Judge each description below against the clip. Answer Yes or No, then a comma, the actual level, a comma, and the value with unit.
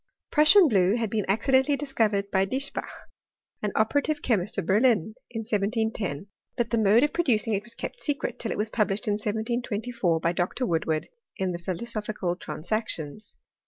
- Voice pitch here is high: Yes, high, 215 Hz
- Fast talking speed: No, average, 165 wpm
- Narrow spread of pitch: No, average, 3.7 semitones